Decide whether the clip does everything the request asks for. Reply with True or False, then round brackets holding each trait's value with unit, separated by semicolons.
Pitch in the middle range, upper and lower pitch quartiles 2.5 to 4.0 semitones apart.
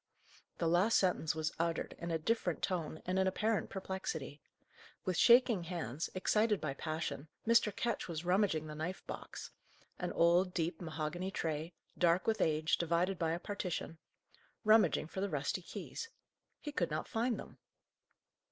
True (175 Hz; 3.5 semitones)